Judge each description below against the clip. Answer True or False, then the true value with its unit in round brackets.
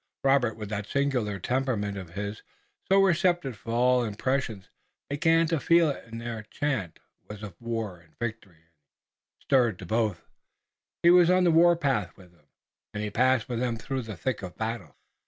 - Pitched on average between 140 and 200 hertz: False (115 Hz)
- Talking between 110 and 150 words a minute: False (175 wpm)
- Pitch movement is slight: False (5.2 semitones)